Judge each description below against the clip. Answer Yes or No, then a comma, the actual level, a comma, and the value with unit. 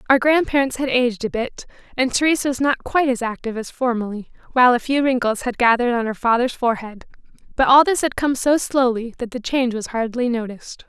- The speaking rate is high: Yes, fast, 210 wpm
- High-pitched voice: Yes, very high, 250 Hz